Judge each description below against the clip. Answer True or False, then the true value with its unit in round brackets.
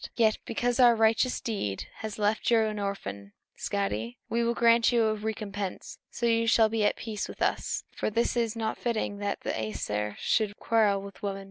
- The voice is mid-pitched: False (215 Hz)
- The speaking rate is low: False (195 wpm)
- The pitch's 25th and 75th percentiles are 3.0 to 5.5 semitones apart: False (2.5 semitones)